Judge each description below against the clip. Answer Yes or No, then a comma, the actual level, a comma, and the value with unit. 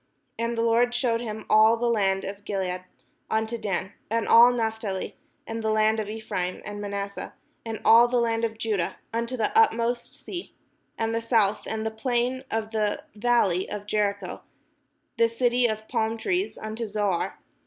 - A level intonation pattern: Yes, narrow, 2.1 semitones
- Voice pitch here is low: No, high, 220 Hz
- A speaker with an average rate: Yes, average, 170 wpm